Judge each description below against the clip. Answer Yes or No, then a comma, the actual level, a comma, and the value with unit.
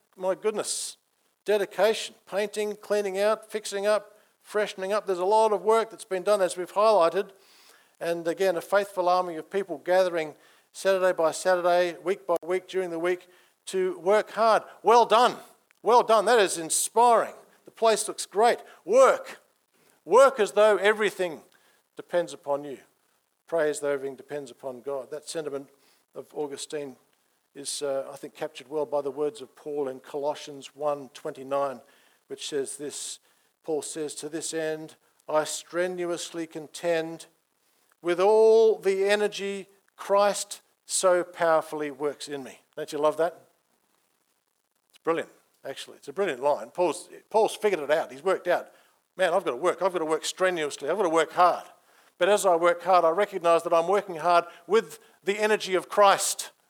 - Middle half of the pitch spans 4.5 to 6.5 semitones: Yes, average, 4.9 semitones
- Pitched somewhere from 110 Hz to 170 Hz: No, medium, 180 Hz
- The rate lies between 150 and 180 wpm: Yes, average, 165 wpm